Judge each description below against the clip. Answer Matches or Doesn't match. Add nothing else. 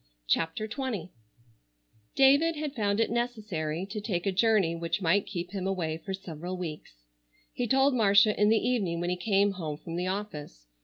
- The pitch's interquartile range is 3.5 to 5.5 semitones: Matches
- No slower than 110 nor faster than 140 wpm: Doesn't match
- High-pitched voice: Matches